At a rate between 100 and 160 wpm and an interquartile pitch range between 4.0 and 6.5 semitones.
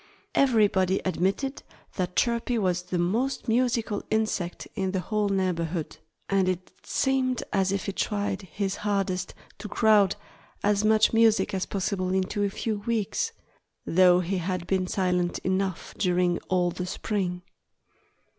No: average, 140 wpm; average, 2.8 semitones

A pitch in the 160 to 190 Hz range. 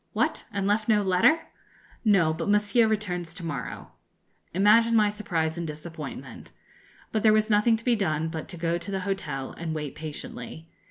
Yes: medium, 185 Hz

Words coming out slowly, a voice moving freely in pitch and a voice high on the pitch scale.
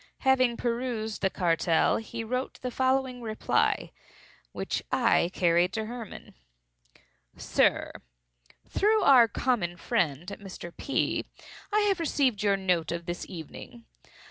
Yes: slow, 115 wpm; wide, 6.5 semitones; high, 220 Hz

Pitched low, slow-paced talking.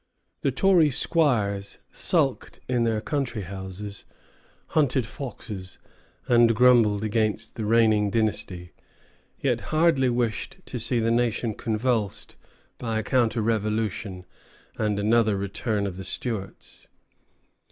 Yes: low, 110 Hz; slow, 115 wpm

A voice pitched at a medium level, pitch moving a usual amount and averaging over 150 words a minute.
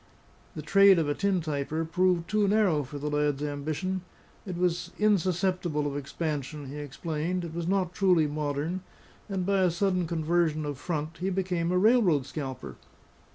Yes: medium, 165 Hz; average, 3.9 semitones; average, 165 wpm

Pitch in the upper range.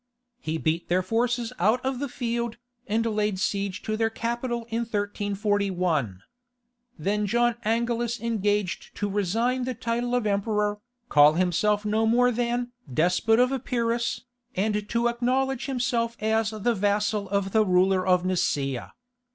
Yes: high, 220 Hz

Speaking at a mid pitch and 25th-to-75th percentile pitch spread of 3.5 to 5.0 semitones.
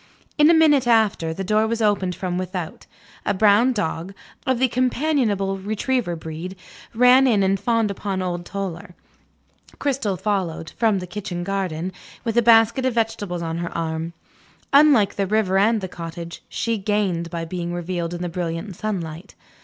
No: high, 195 Hz; average, 4.4 semitones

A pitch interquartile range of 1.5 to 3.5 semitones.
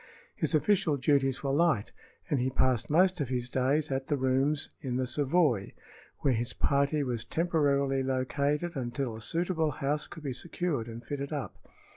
Yes: average, 2.9 semitones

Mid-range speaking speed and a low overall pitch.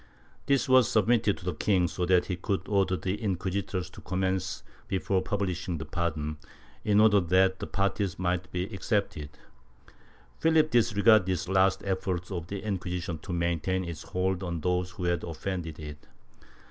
Yes: average, 160 wpm; very low, 95 Hz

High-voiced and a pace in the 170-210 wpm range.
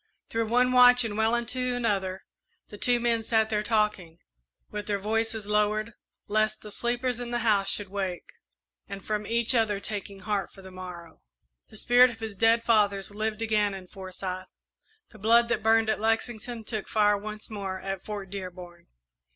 Yes: high, 215 Hz; average, 175 wpm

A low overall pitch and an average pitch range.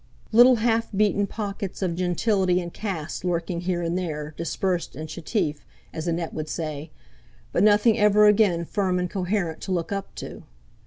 No: medium, 180 Hz; average, 3.6 semitones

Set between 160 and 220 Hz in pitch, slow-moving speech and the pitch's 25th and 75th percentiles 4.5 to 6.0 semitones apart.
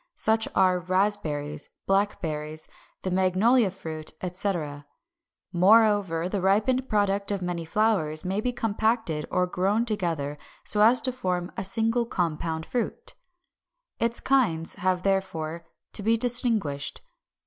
Yes: high, 190 Hz; slow, 125 wpm; average, 4.9 semitones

